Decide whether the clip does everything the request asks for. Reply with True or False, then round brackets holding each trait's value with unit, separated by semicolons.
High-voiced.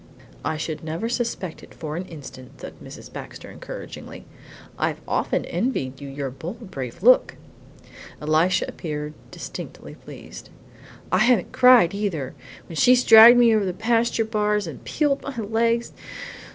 True (195 Hz)